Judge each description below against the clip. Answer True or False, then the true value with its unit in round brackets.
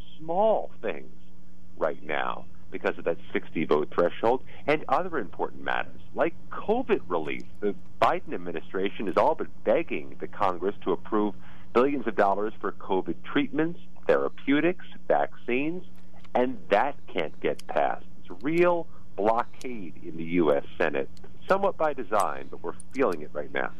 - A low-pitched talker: True (105 Hz)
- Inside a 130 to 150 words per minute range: True (145 wpm)